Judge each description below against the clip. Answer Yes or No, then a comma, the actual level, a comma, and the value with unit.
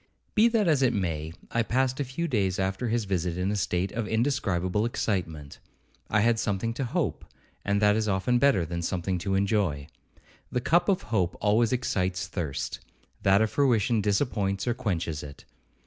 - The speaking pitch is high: No, low, 105 Hz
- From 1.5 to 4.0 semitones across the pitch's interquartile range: No, average, 4.5 semitones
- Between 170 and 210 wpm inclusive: Yes, average, 180 wpm